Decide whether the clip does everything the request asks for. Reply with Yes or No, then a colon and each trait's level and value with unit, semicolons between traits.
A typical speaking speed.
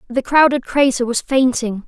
Yes: average, 160 wpm